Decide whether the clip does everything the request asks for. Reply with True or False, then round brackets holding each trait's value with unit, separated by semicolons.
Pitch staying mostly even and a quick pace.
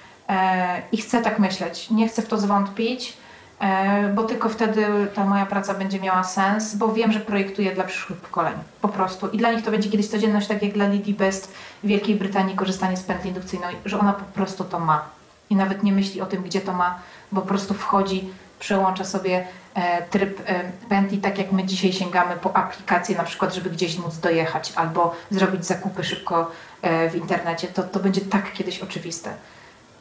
True (1.8 semitones; 190 wpm)